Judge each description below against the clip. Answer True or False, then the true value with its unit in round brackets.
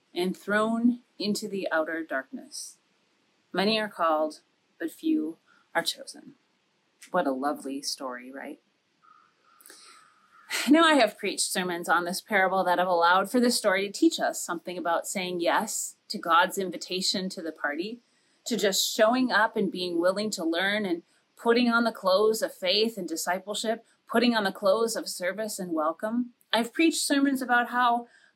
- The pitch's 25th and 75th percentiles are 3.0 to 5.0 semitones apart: False (5.4 semitones)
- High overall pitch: True (210 Hz)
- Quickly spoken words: False (160 wpm)